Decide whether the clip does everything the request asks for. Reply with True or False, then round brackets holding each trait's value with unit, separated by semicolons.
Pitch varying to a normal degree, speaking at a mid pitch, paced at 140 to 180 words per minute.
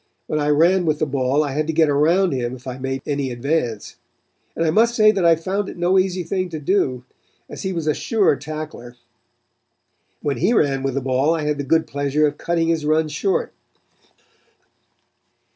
False (3.7 semitones; 155 Hz; 205 wpm)